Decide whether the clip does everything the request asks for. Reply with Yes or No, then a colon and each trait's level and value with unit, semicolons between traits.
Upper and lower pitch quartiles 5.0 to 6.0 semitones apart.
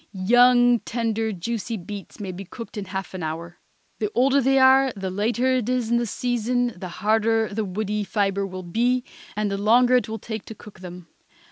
No: average, 3.7 semitones